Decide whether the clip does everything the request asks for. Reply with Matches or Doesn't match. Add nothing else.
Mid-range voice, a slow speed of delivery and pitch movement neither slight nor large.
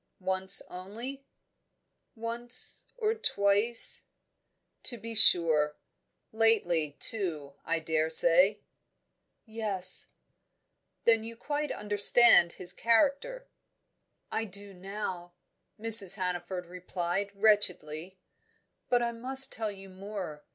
Doesn't match